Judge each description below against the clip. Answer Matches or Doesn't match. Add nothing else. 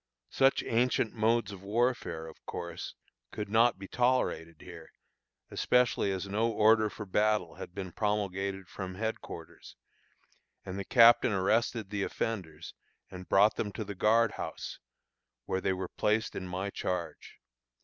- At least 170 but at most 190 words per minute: Doesn't match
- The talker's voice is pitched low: Matches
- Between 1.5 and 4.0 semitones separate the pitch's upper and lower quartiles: Matches